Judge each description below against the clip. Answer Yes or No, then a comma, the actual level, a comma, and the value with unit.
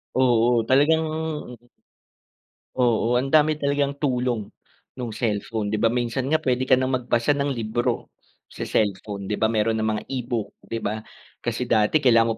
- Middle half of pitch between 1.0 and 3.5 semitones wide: Yes, average, 2.9 semitones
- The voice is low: Yes, low, 120 Hz